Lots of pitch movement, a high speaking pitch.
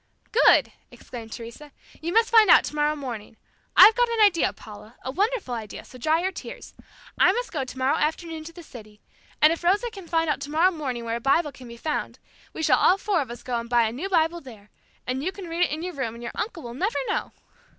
Yes: wide, 6.9 semitones; very high, 305 Hz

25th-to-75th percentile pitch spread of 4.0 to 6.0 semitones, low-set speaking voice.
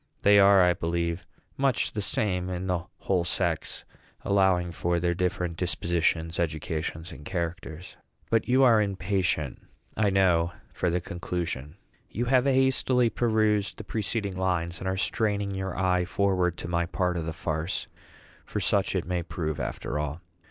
No: average, 2.8 semitones; very low, 90 Hz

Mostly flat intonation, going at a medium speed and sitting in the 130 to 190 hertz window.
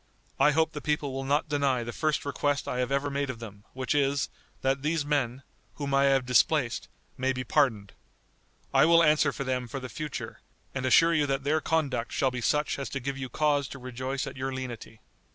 No: narrow, 2.3 semitones; fast, 215 wpm; low, 135 Hz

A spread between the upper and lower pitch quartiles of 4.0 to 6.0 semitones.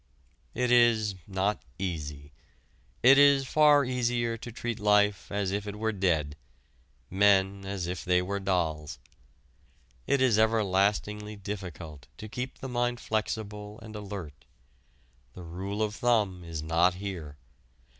No: average, 3.5 semitones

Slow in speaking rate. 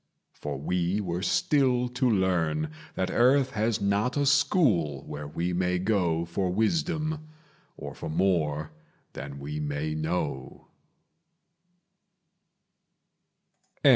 Yes: slow, 110 wpm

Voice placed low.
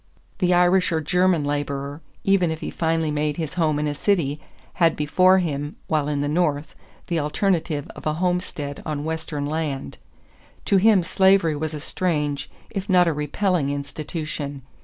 No: medium, 155 Hz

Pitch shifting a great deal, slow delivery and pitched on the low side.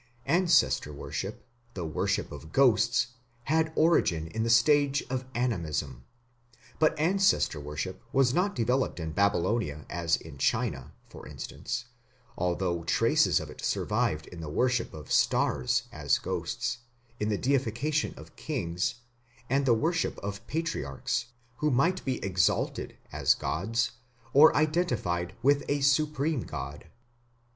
Yes: wide, 8.7 semitones; slow, 130 wpm; low, 120 Hz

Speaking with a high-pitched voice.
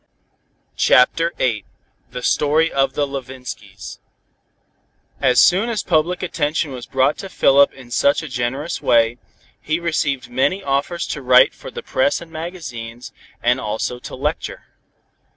No: medium, 140 Hz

